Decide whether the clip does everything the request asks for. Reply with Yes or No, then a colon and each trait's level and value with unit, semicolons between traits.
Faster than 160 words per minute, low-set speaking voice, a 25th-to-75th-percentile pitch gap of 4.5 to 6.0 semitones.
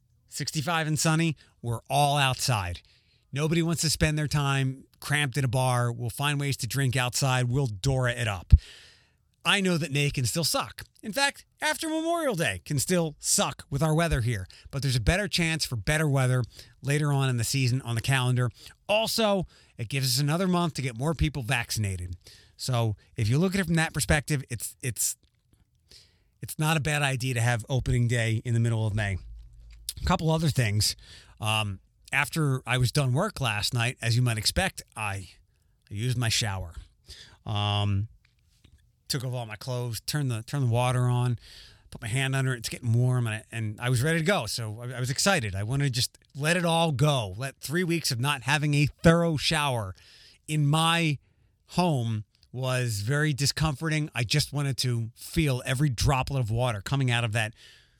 Yes: average, 195 wpm; low, 130 Hz; average, 4.8 semitones